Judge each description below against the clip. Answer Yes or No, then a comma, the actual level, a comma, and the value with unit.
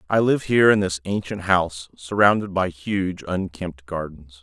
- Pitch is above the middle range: No, very low, 90 Hz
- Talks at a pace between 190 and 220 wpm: No, average, 165 wpm